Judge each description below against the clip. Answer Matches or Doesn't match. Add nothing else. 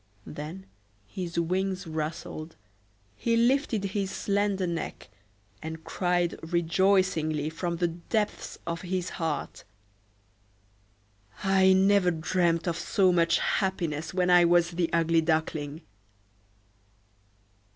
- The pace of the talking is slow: Matches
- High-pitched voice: Doesn't match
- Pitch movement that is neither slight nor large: Matches